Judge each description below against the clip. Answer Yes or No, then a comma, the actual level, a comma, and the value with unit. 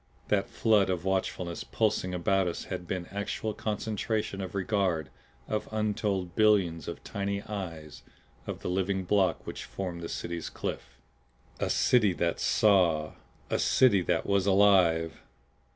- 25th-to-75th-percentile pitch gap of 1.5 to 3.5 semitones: Yes, average, 2.9 semitones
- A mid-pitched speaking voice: No, very low, 95 Hz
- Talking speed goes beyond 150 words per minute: No, average, 140 wpm